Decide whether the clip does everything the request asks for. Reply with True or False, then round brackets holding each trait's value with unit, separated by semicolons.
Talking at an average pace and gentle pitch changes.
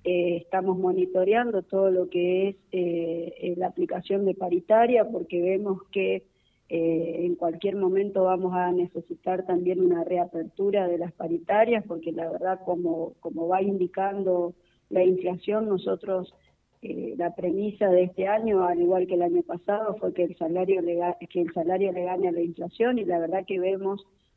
True (165 wpm; 1.8 semitones)